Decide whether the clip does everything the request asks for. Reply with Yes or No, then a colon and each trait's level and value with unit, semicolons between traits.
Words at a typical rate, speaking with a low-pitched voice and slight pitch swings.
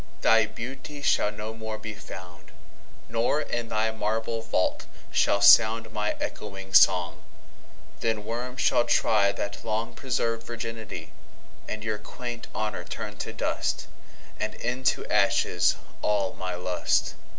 No: slow, 115 wpm; low, 110 Hz; narrow, 2.0 semitones